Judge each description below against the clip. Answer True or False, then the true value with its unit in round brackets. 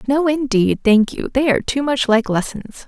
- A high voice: True (250 Hz)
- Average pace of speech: False (210 wpm)